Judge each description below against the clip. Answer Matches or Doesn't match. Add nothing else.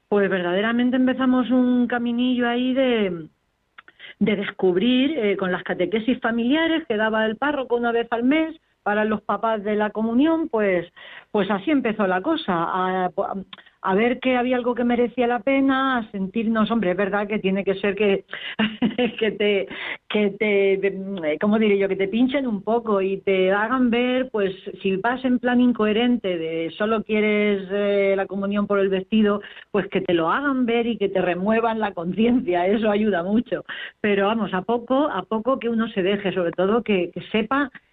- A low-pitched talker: Doesn't match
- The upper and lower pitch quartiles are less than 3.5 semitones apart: Doesn't match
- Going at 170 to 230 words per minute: Matches